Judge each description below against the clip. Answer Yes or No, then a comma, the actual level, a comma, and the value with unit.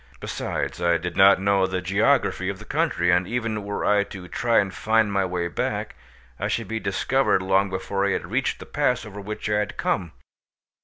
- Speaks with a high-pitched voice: No, low, 100 Hz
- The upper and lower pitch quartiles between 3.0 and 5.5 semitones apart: No, narrow, 2.5 semitones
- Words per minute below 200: No, fast, 205 wpm